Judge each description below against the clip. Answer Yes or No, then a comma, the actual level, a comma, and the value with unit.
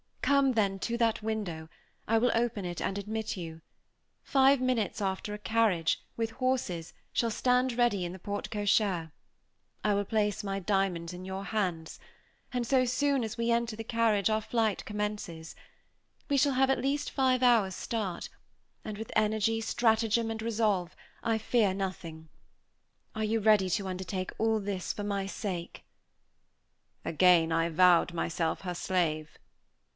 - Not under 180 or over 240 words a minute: No, average, 160 wpm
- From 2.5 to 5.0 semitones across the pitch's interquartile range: Yes, average, 3.8 semitones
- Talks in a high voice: Yes, high, 210 Hz